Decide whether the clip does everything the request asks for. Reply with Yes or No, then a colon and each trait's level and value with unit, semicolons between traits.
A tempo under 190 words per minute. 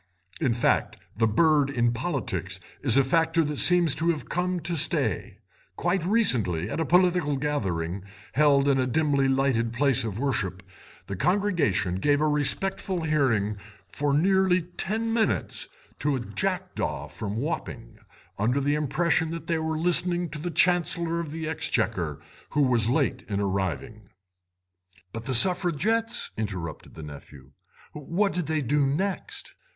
Yes: average, 150 wpm